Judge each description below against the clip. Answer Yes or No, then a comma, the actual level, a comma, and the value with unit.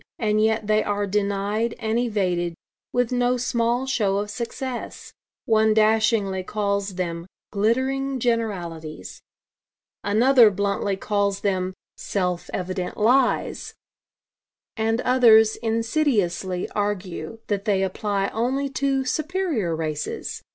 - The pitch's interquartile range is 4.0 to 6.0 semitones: No, average, 3.4 semitones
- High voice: Yes, high, 215 Hz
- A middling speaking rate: No, slow, 110 wpm